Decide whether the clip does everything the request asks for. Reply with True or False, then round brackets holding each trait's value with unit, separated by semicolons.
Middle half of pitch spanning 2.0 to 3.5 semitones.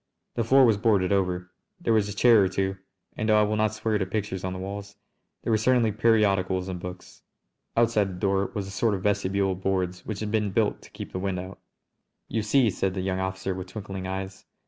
True (2.4 semitones)